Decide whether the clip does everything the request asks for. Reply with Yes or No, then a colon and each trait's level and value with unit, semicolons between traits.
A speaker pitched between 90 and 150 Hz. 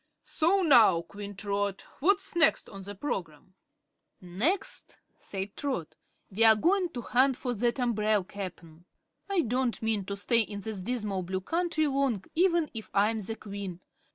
No: high, 220 Hz